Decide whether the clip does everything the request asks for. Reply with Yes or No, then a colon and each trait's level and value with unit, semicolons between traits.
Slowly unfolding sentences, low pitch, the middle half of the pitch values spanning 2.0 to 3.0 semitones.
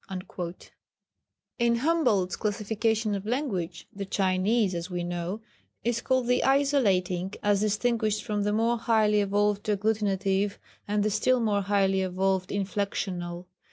No: slow, 130 wpm; high, 205 Hz; average, 2.7 semitones